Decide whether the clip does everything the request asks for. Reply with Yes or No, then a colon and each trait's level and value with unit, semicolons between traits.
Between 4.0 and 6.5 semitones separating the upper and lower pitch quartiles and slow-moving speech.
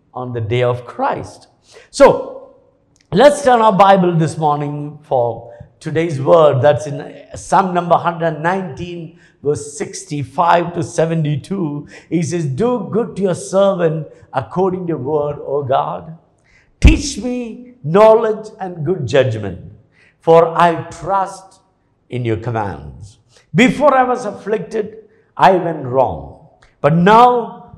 Yes: average, 5.3 semitones; slow, 125 wpm